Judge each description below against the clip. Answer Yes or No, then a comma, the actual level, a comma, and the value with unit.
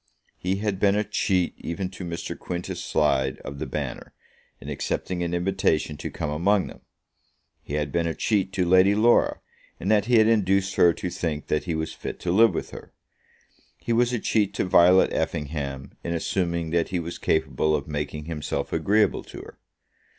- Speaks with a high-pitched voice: No, very low, 85 Hz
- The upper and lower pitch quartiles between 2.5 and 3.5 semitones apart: No, average, 4.0 semitones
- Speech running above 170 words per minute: Yes, average, 190 wpm